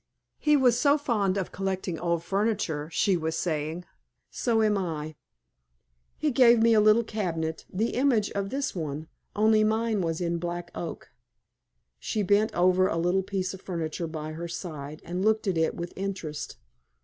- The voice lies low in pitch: No, medium, 185 Hz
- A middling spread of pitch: Yes, average, 4.6 semitones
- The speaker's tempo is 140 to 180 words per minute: Yes, average, 170 wpm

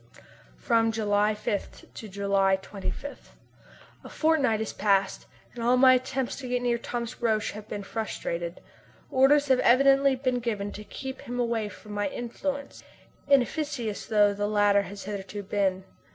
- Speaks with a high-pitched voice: Yes, high, 225 Hz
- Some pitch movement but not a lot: Yes, average, 3.8 semitones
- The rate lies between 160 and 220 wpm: No, average, 150 wpm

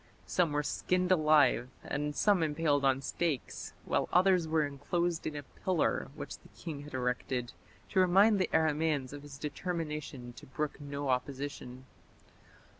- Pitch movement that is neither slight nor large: Yes, average, 3.4 semitones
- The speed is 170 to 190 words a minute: No, average, 150 wpm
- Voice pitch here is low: No, medium, 150 Hz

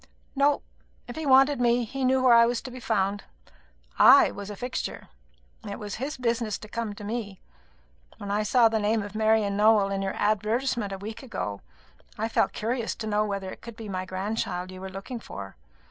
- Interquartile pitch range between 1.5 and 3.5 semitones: Yes, average, 3.1 semitones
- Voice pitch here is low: No, high, 215 Hz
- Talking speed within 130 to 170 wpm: No, fast, 205 wpm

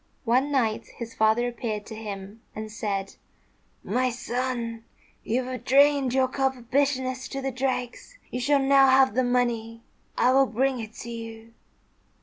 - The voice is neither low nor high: No, high, 245 Hz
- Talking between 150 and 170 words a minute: Yes, average, 160 wpm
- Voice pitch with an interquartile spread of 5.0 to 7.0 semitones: No, narrow, 2.6 semitones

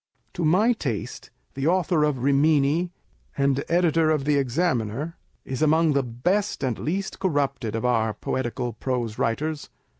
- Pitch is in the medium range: Yes, medium, 145 Hz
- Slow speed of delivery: No, average, 145 wpm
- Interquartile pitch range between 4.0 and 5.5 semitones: Yes, average, 4.6 semitones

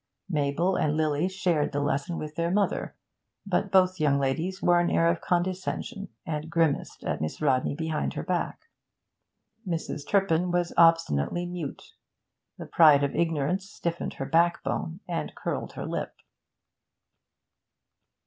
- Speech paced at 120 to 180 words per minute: Yes, average, 140 wpm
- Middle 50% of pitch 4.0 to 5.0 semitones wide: No, average, 3.0 semitones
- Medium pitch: Yes, medium, 165 Hz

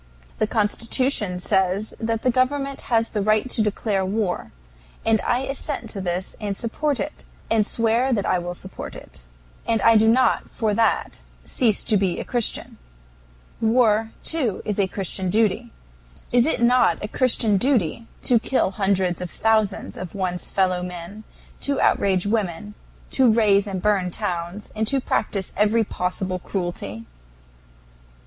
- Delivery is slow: No, average, 155 wpm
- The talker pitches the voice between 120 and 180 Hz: No, high, 210 Hz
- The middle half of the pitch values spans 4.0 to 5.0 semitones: No, average, 3.5 semitones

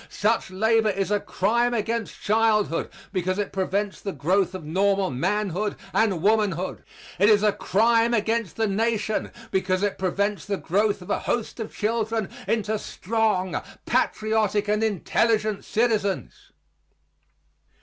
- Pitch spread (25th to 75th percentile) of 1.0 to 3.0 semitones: Yes, narrow, 2.5 semitones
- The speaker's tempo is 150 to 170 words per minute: No, slow, 135 wpm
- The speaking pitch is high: Yes, high, 210 Hz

